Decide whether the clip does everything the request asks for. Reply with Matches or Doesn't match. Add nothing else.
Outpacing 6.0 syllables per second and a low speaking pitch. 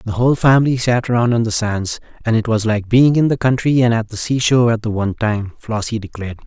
Matches